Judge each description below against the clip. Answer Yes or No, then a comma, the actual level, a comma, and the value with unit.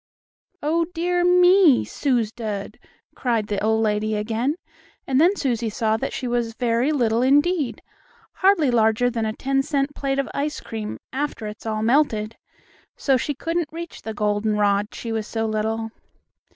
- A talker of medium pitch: No, high, 240 Hz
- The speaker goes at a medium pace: Yes, average, 160 wpm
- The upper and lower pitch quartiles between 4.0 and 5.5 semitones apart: Yes, average, 4.9 semitones